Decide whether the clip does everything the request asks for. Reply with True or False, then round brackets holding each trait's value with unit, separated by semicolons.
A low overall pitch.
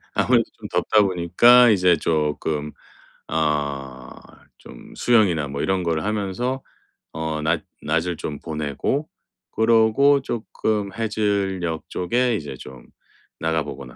True (85 Hz)